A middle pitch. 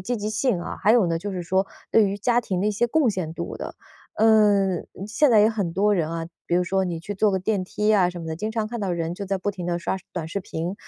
No: high, 195 Hz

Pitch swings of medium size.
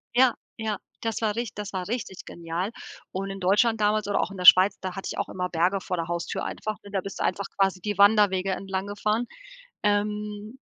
No: narrow, 2.1 semitones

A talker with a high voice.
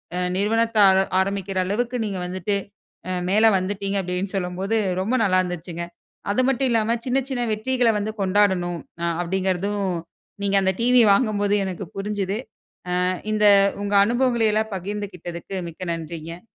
Yes: high, 200 Hz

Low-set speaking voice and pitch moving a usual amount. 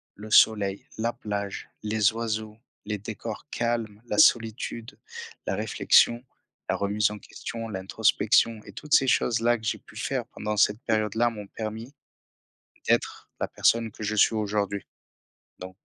No: low, 110 Hz; narrow, 1.9 semitones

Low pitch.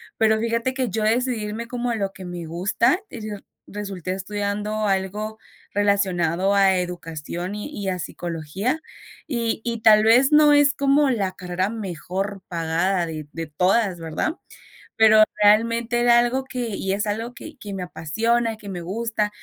No: high, 205 Hz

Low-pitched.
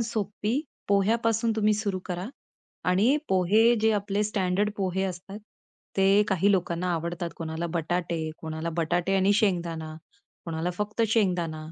No: high, 190 Hz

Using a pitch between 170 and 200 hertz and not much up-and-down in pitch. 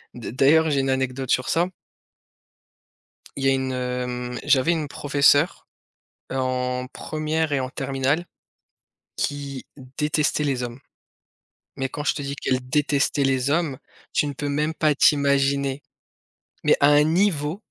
No: medium, 140 Hz; narrow, 2.2 semitones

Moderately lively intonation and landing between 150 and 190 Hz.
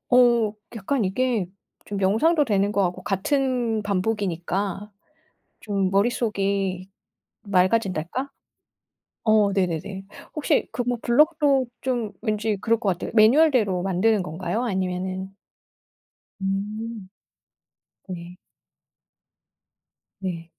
No: average, 3.9 semitones; high, 205 Hz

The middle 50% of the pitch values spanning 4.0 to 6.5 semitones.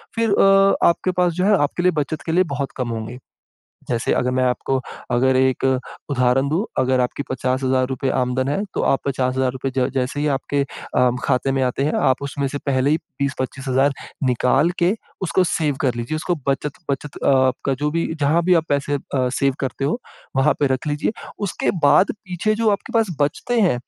No: average, 3.3 semitones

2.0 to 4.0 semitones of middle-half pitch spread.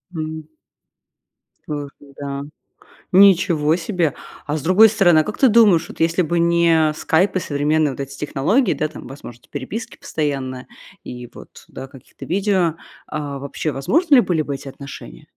No: average, 4.4 semitones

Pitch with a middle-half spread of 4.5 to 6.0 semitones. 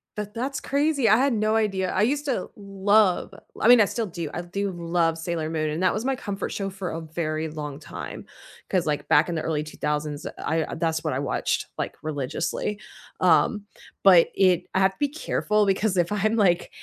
Yes: average, 4.8 semitones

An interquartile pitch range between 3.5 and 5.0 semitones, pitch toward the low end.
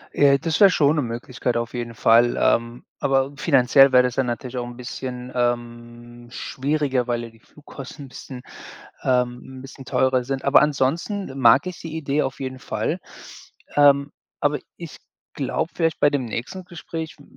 No: average, 2.9 semitones; low, 130 Hz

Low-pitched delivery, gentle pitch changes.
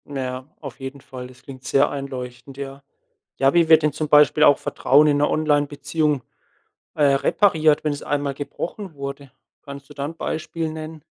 No: medium, 145 Hz; narrow, 2.0 semitones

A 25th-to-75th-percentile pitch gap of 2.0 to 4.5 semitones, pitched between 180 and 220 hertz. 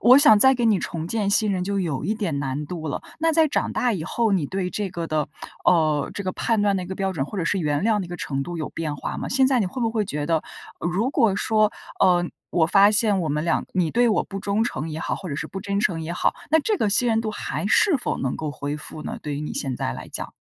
No: wide, 5.4 semitones; high, 190 Hz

